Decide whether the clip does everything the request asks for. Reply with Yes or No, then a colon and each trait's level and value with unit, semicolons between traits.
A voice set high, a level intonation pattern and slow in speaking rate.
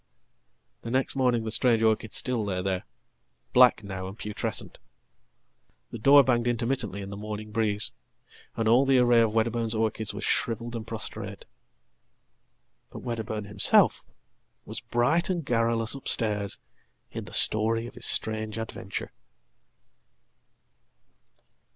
No: low, 115 Hz; narrow, 2.2 semitones; slow, 120 wpm